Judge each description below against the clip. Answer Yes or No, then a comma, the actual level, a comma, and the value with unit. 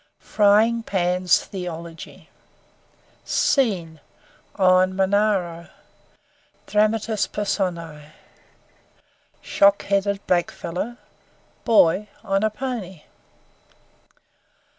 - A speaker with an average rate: No, slow, 60 wpm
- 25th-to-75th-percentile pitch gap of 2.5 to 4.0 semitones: Yes, average, 3.3 semitones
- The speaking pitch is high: Yes, high, 195 Hz